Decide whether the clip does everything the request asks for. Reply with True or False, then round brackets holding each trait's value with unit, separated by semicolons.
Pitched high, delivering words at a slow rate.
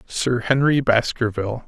False (120 Hz; 105 wpm)